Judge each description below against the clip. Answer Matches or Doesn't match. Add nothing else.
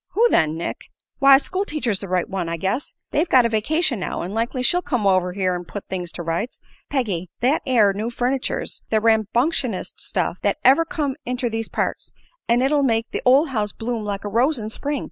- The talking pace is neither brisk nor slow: Doesn't match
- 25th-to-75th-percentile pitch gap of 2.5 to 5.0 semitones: Doesn't match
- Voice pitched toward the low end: Doesn't match